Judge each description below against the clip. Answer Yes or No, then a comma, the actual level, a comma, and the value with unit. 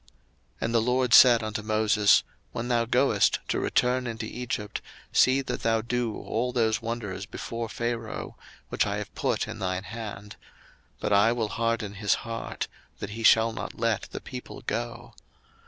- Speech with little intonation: Yes, narrow, 1.6 semitones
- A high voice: No, low, 115 Hz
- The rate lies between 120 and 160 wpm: No, average, 170 wpm